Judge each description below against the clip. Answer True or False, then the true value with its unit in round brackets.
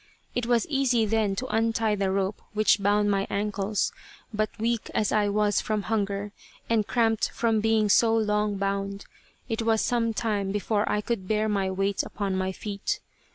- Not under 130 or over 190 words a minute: True (175 wpm)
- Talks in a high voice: True (210 Hz)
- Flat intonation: True (2.0 semitones)